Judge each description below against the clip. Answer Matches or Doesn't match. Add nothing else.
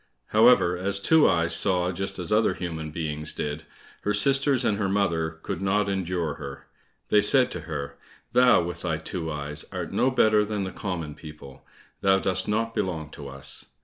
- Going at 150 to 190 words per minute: Matches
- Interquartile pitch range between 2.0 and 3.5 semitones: Doesn't match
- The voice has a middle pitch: Doesn't match